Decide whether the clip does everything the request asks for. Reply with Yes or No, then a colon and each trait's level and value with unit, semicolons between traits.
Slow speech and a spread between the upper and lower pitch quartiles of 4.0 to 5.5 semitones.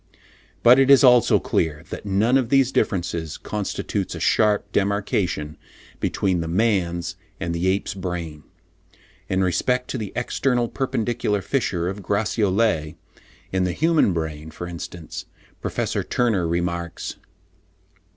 Yes: slow, 130 wpm; average, 5.2 semitones